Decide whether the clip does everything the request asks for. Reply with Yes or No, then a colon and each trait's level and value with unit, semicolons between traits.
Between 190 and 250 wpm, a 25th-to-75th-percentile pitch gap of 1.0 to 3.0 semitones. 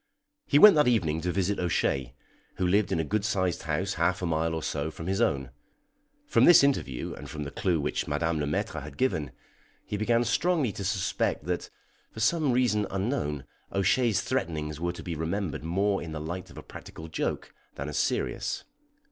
No: average, 195 wpm; average, 4.9 semitones